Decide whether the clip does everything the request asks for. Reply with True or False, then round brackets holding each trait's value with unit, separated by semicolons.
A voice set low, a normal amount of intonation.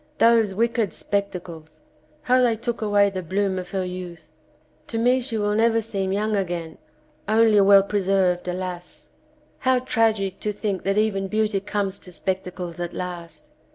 False (195 Hz; 3.1 semitones)